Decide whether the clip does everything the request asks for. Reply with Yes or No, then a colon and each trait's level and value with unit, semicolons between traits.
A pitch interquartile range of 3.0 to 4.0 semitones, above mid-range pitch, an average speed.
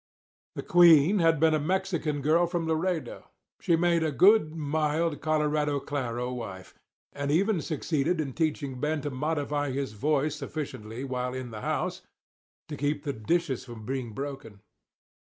No: average, 3.4 semitones; medium, 150 Hz; average, 155 wpm